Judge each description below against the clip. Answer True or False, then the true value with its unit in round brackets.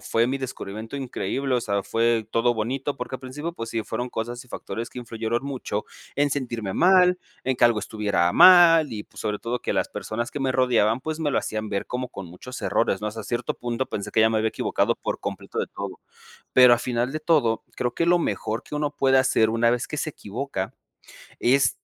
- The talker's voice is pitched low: True (120 Hz)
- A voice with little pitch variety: False (3.4 semitones)